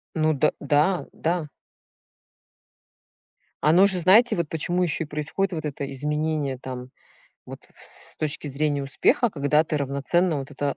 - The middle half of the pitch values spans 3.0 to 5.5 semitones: Yes, average, 3.4 semitones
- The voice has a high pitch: No, medium, 150 Hz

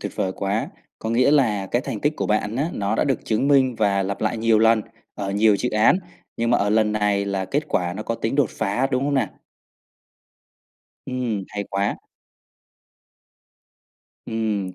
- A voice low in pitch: Yes, low, 110 Hz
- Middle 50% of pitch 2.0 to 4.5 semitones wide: Yes, average, 3.6 semitones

